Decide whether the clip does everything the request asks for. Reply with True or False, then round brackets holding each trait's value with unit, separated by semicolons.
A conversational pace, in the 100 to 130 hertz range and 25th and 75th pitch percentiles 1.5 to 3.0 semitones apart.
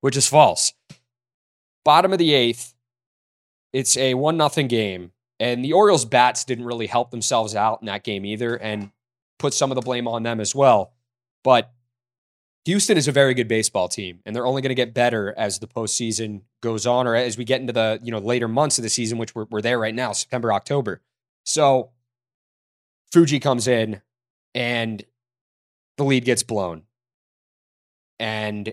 True (180 wpm; 120 Hz; 2.6 semitones)